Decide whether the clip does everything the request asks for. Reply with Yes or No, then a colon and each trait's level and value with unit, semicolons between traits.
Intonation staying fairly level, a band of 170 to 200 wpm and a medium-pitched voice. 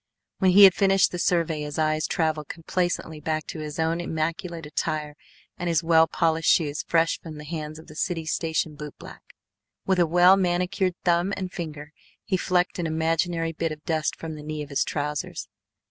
Yes: narrow, 2.3 semitones; average, 190 wpm; medium, 165 Hz